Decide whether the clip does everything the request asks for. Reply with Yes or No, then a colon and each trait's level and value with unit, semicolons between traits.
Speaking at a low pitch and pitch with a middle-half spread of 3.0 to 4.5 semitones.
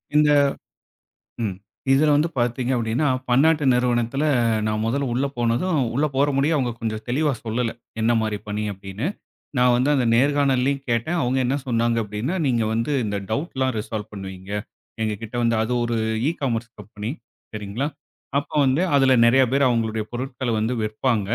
Yes: low, 120 Hz; average, 3.5 semitones